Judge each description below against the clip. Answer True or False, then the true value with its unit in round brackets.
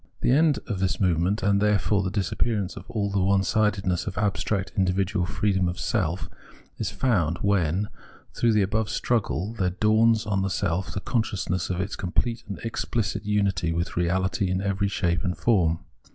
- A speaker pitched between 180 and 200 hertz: False (100 Hz)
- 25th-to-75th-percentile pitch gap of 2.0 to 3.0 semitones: True (2.5 semitones)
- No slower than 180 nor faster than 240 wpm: False (170 wpm)